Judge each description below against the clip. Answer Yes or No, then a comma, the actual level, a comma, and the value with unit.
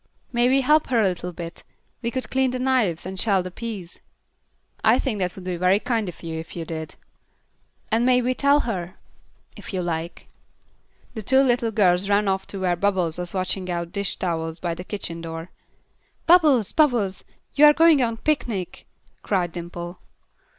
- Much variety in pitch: Yes, wide, 5.8 semitones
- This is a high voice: Yes, high, 195 Hz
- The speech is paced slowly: No, average, 180 wpm